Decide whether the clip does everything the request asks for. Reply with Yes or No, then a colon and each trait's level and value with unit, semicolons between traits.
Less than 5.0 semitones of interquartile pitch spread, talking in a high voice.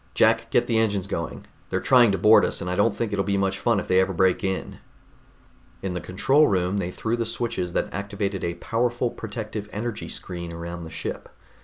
No: average, 3.7 semitones; low, 100 Hz